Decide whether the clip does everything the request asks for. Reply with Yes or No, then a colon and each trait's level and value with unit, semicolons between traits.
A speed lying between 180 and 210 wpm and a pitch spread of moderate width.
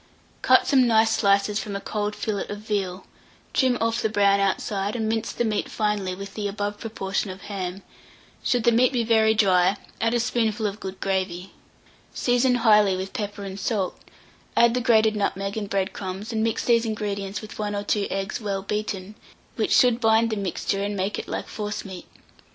No: average, 190 wpm; narrow, 2.1 semitones